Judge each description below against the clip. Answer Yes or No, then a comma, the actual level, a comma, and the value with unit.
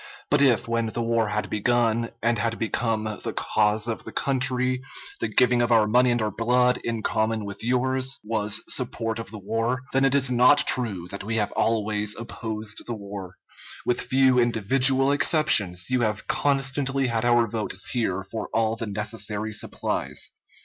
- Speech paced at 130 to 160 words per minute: No, average, 175 wpm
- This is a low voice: Yes, low, 115 Hz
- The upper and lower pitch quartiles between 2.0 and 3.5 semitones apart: Yes, average, 2.7 semitones